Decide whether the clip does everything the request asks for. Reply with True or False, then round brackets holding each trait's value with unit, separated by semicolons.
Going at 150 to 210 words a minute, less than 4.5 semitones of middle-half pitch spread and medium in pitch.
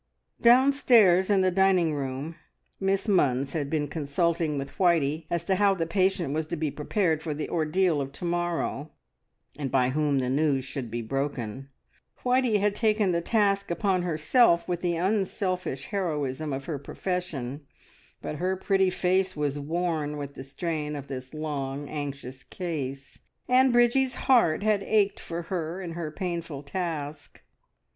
False (160 wpm; 4.8 semitones; 165 Hz)